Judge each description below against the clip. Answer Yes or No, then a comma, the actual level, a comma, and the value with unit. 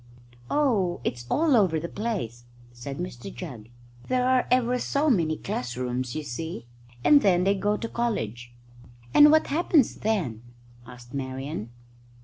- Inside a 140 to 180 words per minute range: Yes, average, 145 wpm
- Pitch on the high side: No, medium, 175 Hz